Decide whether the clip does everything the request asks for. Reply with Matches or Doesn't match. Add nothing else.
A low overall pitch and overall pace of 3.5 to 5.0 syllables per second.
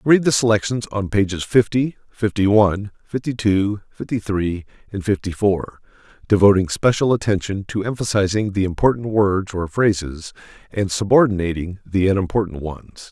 Matches